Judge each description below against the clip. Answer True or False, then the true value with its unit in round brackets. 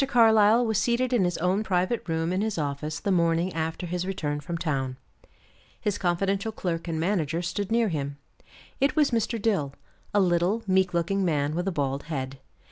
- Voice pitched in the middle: True (180 Hz)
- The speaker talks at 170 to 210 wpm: True (185 wpm)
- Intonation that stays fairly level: False (4.4 semitones)